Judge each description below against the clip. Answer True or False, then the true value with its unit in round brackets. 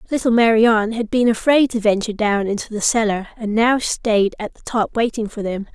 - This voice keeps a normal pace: False (210 wpm)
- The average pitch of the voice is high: True (220 Hz)